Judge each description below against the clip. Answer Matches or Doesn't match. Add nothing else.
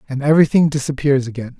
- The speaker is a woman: Doesn't match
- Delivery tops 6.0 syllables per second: Matches